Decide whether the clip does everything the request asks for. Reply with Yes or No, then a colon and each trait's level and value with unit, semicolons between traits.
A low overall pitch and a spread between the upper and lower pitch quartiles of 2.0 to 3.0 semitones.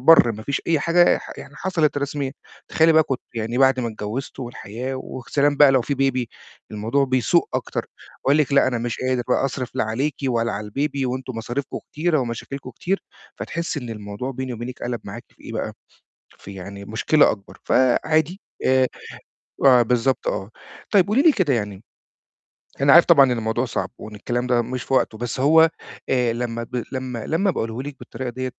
No: low, 130 Hz; average, 3.4 semitones